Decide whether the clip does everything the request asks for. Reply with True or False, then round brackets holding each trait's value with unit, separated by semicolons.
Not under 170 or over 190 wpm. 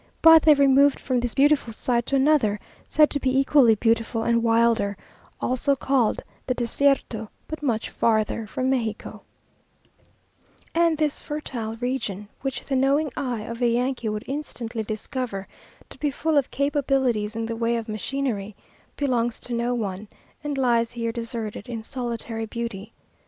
False (155 wpm)